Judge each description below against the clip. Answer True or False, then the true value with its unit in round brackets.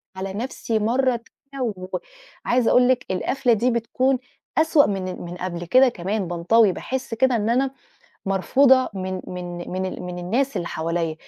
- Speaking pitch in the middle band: False (220 Hz)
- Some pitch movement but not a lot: False (5.8 semitones)